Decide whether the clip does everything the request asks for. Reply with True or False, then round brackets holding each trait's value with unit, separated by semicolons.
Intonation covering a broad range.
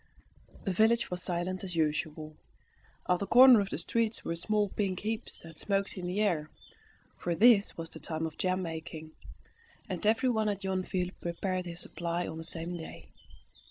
False (3.8 semitones)